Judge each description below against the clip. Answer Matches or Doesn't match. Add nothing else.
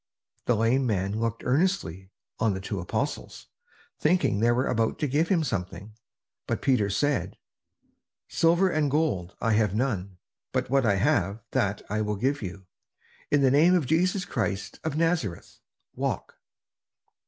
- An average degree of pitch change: Doesn't match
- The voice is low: Matches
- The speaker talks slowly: Doesn't match